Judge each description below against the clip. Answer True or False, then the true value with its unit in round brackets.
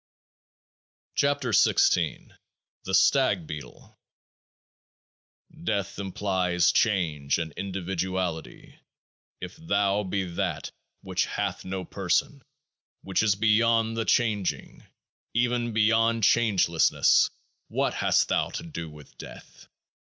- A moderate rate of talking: False (105 wpm)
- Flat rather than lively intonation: False (3.9 semitones)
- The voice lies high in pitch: False (100 Hz)